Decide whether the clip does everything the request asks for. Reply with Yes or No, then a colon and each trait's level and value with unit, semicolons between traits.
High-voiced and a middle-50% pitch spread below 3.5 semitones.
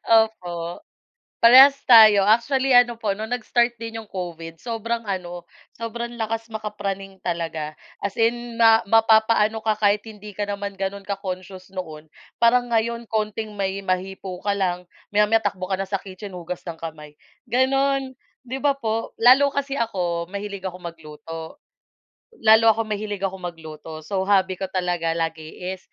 No: high, 205 Hz; average, 3.8 semitones